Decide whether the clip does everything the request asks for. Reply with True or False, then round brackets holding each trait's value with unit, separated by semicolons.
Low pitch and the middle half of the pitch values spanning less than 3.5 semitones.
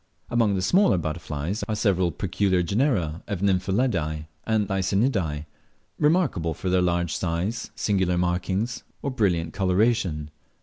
False (95 Hz; 4.0 semitones)